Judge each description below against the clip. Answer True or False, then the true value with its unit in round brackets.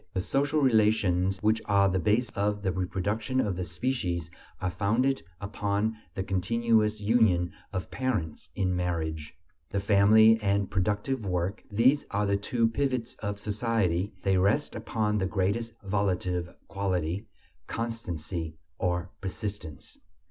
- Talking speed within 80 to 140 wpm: True (135 wpm)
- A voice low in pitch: True (100 Hz)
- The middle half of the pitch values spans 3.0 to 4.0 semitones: True (3.4 semitones)